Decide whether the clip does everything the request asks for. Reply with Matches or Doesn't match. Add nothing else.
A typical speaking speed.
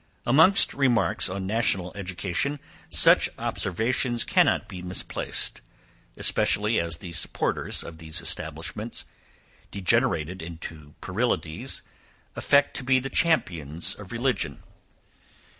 Doesn't match